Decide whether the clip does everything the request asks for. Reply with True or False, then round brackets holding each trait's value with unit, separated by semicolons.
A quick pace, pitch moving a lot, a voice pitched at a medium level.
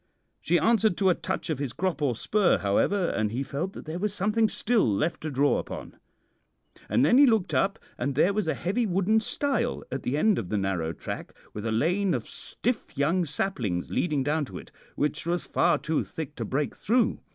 True (210 wpm; 6.7 semitones; 170 Hz)